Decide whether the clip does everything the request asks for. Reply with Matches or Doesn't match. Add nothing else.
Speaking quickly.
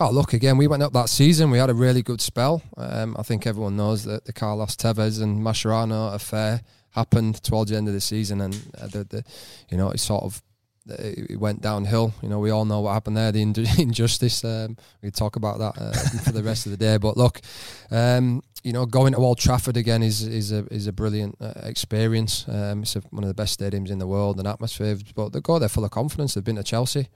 Matches